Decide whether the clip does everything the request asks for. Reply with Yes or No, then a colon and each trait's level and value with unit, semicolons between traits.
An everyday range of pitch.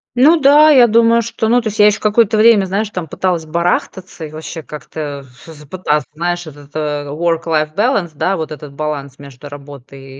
No: wide, 6.2 semitones